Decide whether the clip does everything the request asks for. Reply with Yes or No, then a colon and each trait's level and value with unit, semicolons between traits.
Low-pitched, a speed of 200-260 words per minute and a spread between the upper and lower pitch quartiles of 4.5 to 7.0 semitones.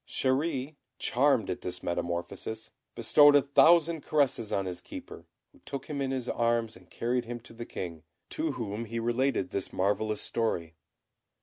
No: low, 115 Hz; average, 165 wpm; average, 5.3 semitones